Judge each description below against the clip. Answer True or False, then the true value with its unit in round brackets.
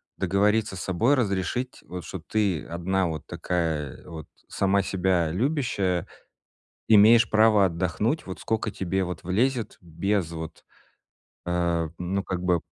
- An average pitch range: True (3.6 semitones)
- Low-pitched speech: True (95 Hz)